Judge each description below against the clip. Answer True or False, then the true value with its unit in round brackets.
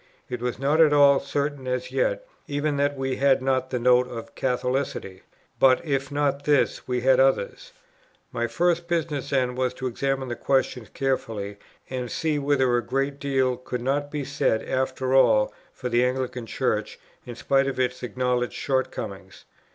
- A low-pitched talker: True (130 Hz)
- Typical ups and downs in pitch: False (2.1 semitones)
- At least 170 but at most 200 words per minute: True (175 wpm)